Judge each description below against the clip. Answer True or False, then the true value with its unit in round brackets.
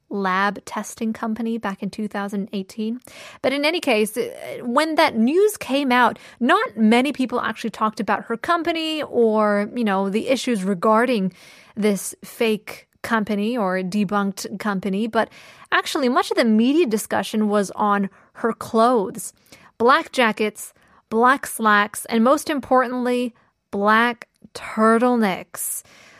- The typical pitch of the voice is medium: False (225 Hz)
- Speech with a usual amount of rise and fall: True (3.3 semitones)